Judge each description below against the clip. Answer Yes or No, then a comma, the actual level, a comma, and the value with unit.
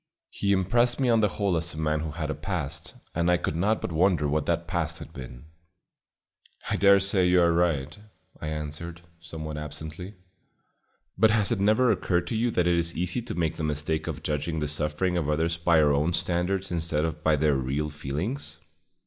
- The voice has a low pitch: Yes, very low, 85 Hz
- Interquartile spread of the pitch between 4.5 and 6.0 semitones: No, average, 3.6 semitones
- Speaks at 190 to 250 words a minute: Yes, fast, 205 wpm